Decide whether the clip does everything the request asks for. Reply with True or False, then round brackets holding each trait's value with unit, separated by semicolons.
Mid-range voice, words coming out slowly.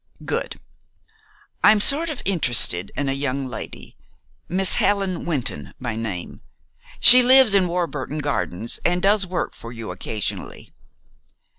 True (165 Hz; 130 wpm)